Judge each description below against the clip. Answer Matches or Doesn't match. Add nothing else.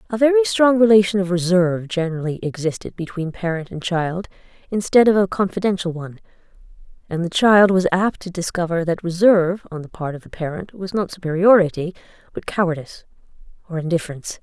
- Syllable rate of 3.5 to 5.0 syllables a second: Doesn't match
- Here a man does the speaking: Doesn't match